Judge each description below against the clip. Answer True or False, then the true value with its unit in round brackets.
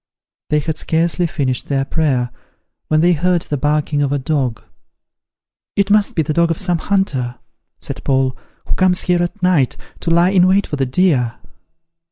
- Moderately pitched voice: True (160 Hz)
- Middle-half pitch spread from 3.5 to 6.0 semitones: True (4.6 semitones)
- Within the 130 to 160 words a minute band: False (180 wpm)